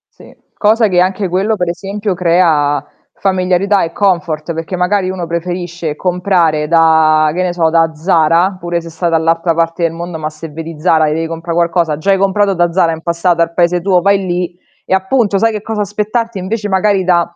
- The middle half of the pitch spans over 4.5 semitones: No, narrow, 2.6 semitones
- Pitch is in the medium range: Yes, medium, 175 Hz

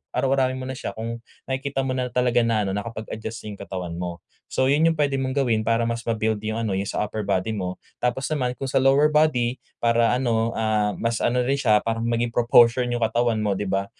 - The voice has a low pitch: Yes, low, 115 Hz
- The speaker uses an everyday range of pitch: Yes, average, 3.0 semitones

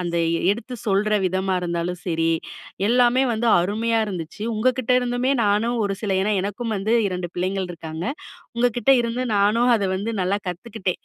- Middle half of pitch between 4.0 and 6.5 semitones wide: Yes, average, 4.3 semitones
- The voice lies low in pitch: No, high, 205 Hz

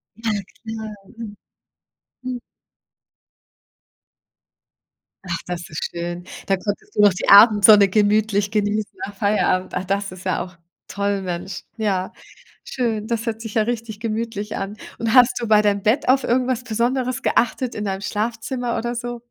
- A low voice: No, high, 215 Hz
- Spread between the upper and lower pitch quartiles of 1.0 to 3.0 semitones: Yes, average, 2.7 semitones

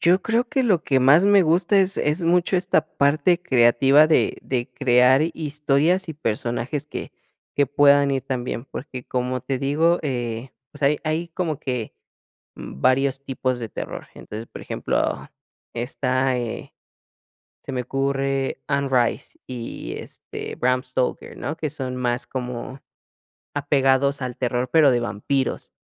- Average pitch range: Yes, average, 3.4 semitones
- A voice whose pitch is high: No, low, 135 Hz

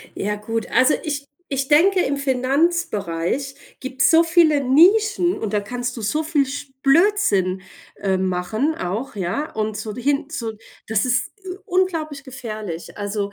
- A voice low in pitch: No, very high, 265 Hz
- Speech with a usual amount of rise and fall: No, wide, 6.6 semitones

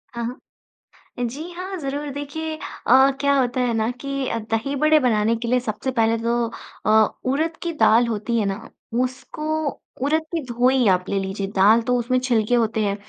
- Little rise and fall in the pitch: No, average, 4.0 semitones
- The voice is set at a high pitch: Yes, very high, 250 Hz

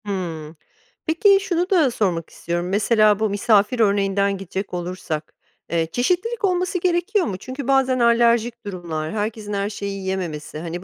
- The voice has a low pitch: No, high, 205 Hz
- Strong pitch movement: Yes, wide, 5.8 semitones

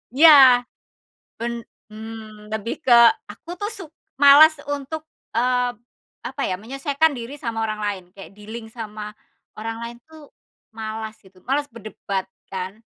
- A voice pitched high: Yes, high, 230 Hz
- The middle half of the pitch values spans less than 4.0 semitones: No, average, 4.4 semitones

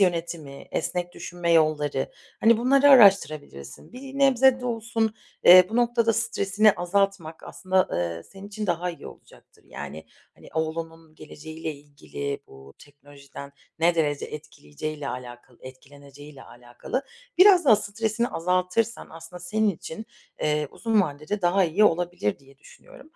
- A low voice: No, medium, 170 Hz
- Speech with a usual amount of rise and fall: No, wide, 6.8 semitones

